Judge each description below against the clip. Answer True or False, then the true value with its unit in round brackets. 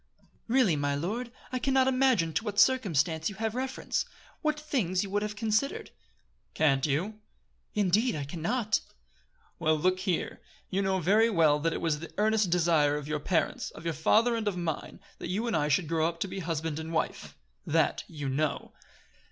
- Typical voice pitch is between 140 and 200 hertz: True (185 Hz)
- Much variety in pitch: True (5.7 semitones)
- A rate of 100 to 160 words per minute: False (195 wpm)